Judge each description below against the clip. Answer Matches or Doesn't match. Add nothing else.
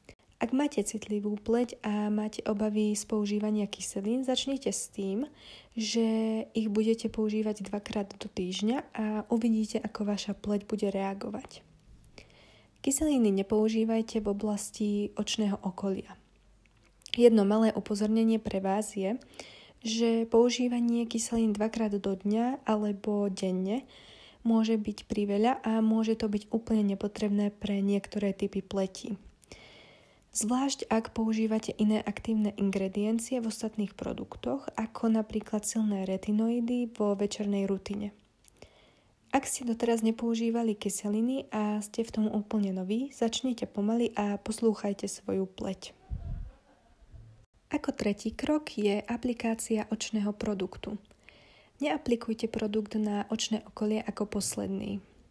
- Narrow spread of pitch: Matches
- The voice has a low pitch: Doesn't match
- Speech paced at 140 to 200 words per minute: Doesn't match